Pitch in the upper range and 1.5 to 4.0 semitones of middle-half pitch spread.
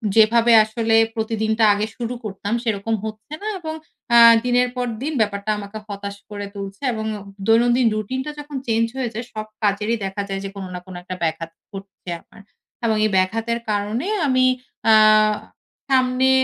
Yes: high, 220 Hz; average, 2.9 semitones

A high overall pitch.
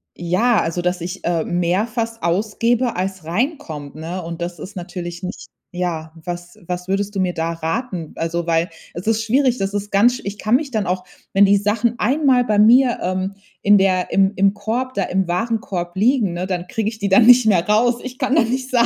Yes: high, 195 Hz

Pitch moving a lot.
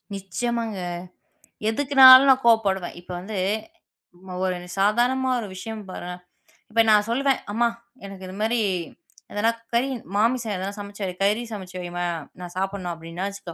No: average, 3.9 semitones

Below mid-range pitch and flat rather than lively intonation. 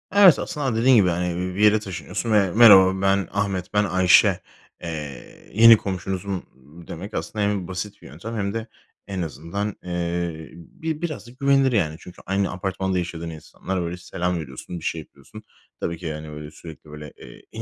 No: very low, 95 Hz; average, 3.6 semitones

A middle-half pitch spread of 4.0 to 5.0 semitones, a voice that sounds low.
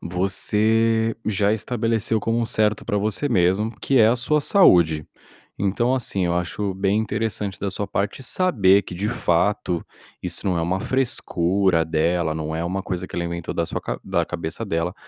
Yes: average, 4.4 semitones; low, 100 Hz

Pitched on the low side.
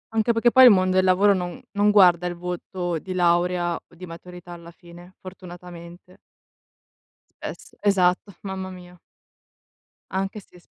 No: medium, 180 Hz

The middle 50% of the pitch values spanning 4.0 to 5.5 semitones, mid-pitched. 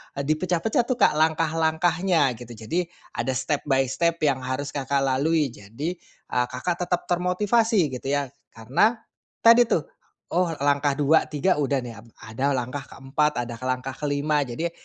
Yes: average, 4.4 semitones; medium, 145 Hz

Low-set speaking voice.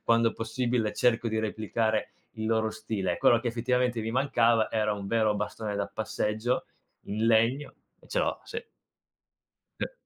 Yes: low, 110 Hz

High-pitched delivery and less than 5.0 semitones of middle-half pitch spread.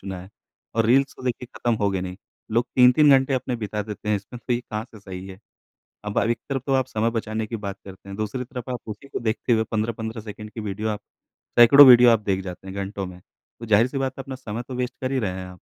No: low, 110 Hz; average, 3.6 semitones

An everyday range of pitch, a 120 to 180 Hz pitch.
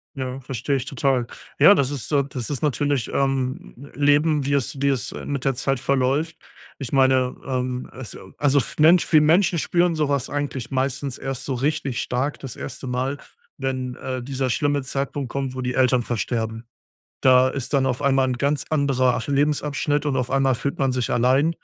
No: narrow, 1.9 semitones; low, 135 Hz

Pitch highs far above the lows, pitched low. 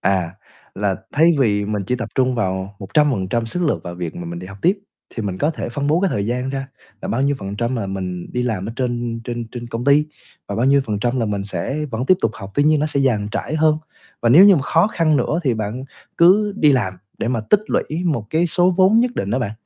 Yes: wide, 6.7 semitones; low, 120 Hz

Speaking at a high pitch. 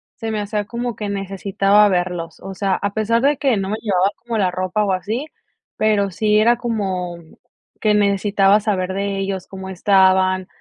Yes: high, 200 Hz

